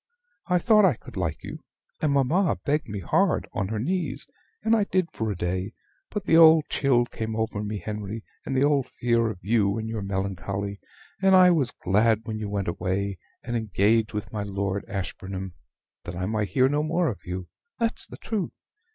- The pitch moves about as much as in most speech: No, wide, 7.0 semitones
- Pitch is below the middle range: Yes, low, 110 Hz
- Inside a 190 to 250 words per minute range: Yes, average, 195 wpm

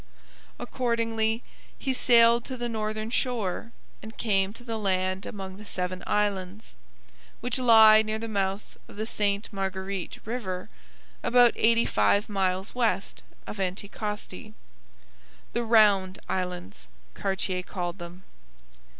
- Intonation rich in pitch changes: No, average, 3.3 semitones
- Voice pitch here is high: Yes, high, 210 Hz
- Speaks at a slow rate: Yes, slow, 125 wpm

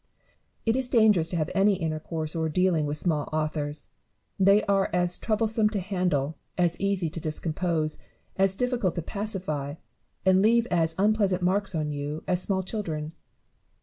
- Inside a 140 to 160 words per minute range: Yes, average, 155 wpm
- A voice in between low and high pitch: Yes, medium, 180 Hz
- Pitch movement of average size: Yes, average, 4.2 semitones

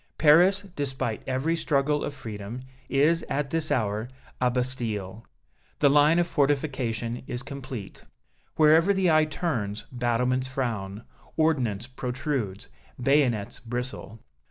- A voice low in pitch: Yes, low, 130 Hz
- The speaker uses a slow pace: Yes, slow, 115 wpm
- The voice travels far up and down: No, average, 4.3 semitones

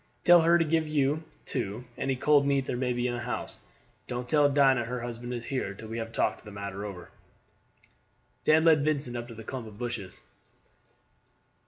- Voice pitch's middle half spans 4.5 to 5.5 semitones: No, average, 3.9 semitones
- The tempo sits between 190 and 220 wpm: Yes, average, 195 wpm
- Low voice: Yes, low, 125 Hz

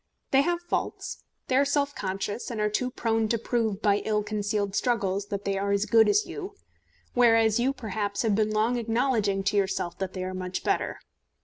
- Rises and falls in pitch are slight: No, average, 3.2 semitones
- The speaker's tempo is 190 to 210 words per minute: Yes, average, 200 wpm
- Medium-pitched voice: No, high, 215 Hz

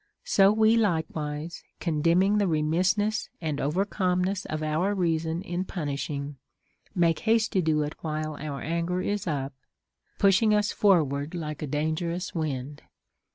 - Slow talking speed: No, average, 145 wpm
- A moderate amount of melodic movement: Yes, average, 3.9 semitones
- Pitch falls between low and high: Yes, medium, 165 Hz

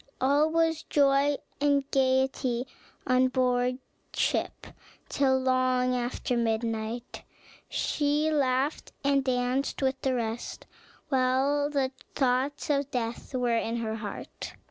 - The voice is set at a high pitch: Yes, very high, 260 Hz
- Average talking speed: No, slow, 115 wpm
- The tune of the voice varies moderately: No, narrow, 2.2 semitones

